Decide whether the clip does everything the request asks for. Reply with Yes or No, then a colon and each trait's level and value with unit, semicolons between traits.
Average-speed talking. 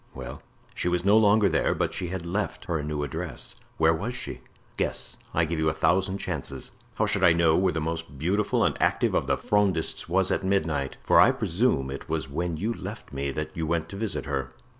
No: fast, 220 wpm